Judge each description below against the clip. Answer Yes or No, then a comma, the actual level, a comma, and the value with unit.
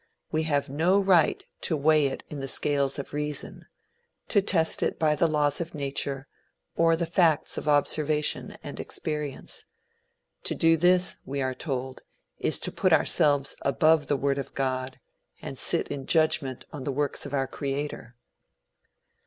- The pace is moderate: Yes, average, 160 wpm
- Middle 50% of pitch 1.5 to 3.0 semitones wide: Yes, narrow, 2.5 semitones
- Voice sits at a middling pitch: Yes, medium, 145 Hz